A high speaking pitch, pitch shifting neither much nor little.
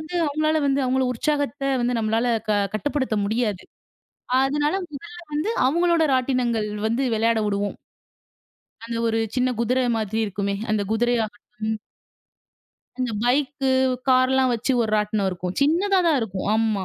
Yes: high, 245 Hz; average, 4.4 semitones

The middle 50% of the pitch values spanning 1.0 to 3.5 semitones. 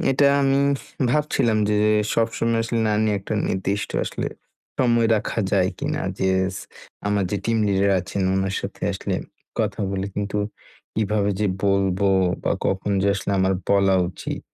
Yes: average, 2.7 semitones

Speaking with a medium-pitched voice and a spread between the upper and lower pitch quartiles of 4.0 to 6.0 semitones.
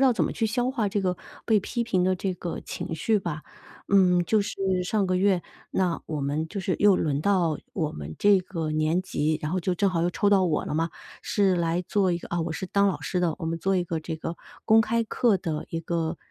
No: medium, 180 Hz; average, 3.6 semitones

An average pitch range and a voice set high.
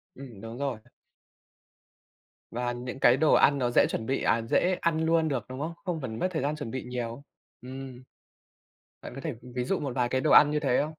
No: average, 3.6 semitones; low, 130 Hz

